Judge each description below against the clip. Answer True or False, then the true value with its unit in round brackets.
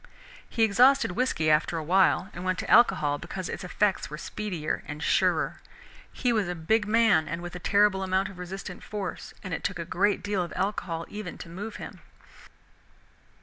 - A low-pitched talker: False (185 Hz)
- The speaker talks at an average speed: True (190 wpm)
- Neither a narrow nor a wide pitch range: True (3.4 semitones)